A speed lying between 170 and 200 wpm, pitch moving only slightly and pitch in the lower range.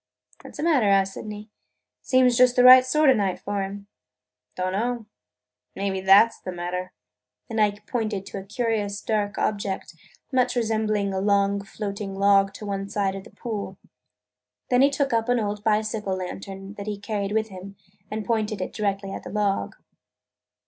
No: average, 180 wpm; narrow, 2.3 semitones; high, 205 Hz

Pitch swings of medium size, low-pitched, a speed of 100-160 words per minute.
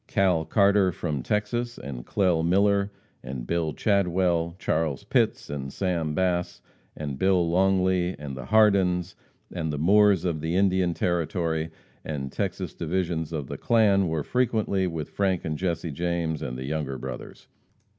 Yes: average, 3.5 semitones; very low, 85 Hz; average, 150 wpm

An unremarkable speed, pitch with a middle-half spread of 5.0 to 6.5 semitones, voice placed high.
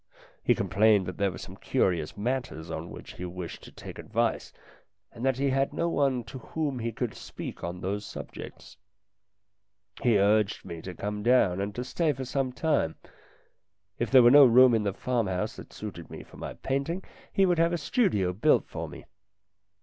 No: average, 190 wpm; wide, 5.6 semitones; low, 115 Hz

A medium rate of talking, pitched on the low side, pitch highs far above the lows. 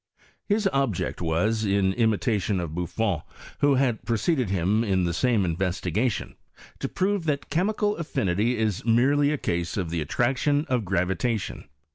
Yes: average, 150 wpm; low, 110 Hz; wide, 6.5 semitones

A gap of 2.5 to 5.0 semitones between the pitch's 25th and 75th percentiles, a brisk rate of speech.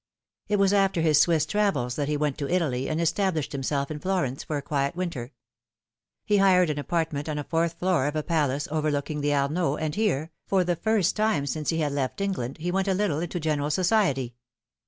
Yes: average, 4.2 semitones; fast, 210 wpm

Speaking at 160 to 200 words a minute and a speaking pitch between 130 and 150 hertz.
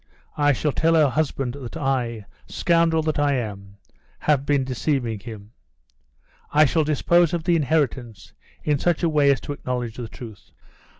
Yes: average, 165 wpm; medium, 140 Hz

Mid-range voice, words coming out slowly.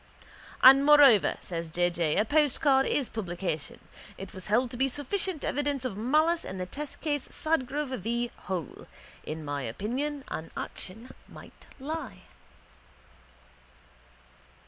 No: very high, 250 Hz; slow, 125 wpm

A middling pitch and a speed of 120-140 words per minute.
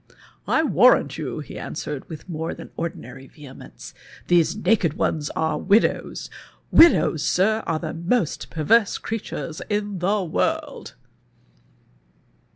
Yes: medium, 170 Hz; slow, 135 wpm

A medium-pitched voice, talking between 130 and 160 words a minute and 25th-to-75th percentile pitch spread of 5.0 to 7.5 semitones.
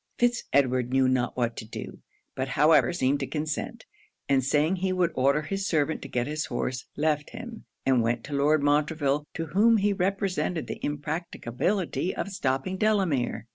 No: medium, 150 Hz; average, 175 wpm; wide, 5.5 semitones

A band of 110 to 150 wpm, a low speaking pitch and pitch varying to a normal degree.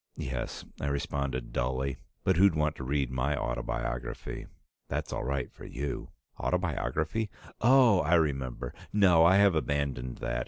Yes: average, 145 wpm; very low, 70 Hz; average, 4.9 semitones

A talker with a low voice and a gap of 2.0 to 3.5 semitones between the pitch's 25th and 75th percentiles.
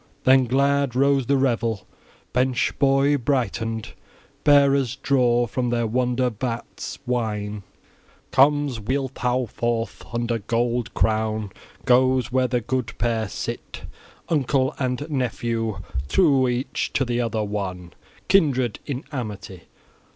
Yes: low, 125 Hz; average, 2.8 semitones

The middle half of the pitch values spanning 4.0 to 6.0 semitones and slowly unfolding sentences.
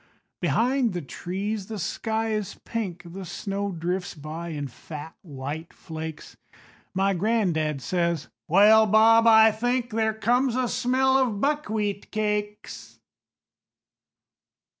Yes: average, 4.7 semitones; slow, 120 wpm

